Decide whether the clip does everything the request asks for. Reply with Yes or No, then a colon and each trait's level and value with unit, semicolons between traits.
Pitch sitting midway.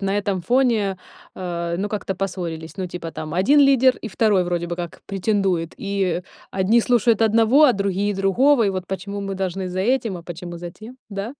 No: high, 195 Hz